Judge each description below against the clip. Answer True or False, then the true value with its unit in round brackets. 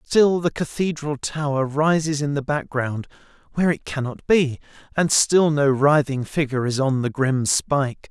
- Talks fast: False (165 wpm)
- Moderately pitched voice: True (145 Hz)